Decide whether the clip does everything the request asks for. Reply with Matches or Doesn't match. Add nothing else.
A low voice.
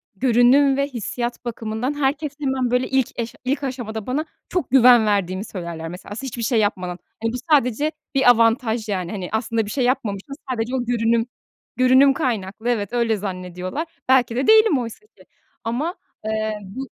Doesn't match